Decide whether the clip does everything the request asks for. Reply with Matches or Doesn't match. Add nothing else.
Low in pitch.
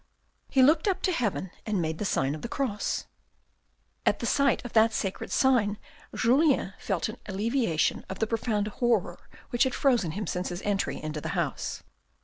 Doesn't match